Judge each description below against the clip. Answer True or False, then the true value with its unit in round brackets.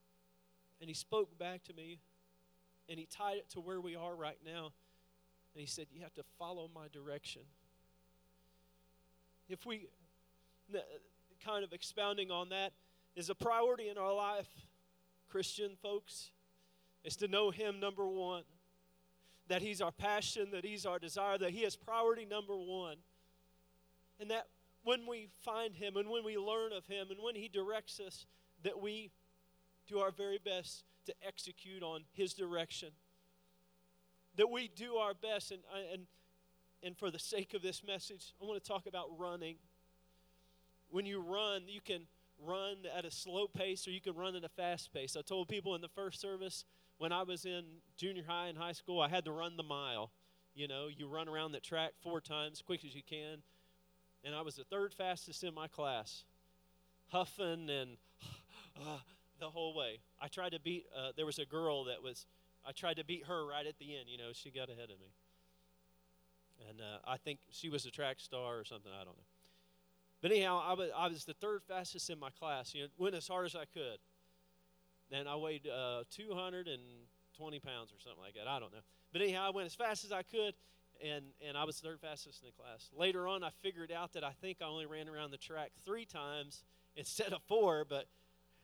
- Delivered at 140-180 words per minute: False (195 wpm)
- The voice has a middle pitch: True (160 Hz)